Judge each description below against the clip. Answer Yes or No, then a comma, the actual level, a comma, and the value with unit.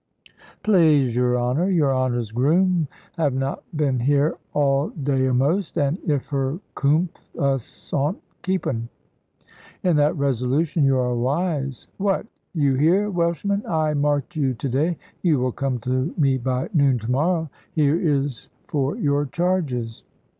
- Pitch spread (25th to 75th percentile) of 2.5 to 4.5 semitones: Yes, average, 3.8 semitones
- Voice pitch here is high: No, medium, 140 Hz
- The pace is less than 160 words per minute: Yes, average, 145 wpm